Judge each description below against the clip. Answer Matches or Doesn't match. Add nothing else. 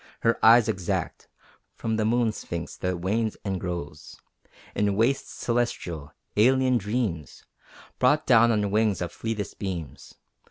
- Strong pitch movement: Doesn't match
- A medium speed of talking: Doesn't match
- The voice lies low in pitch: Matches